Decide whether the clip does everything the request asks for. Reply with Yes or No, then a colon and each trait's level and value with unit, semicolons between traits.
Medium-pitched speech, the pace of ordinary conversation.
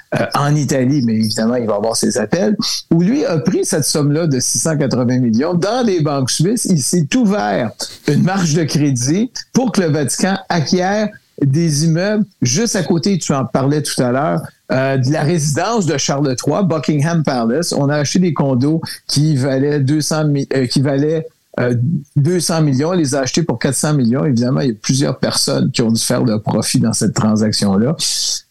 Yes: medium, 150 Hz; average, 195 wpm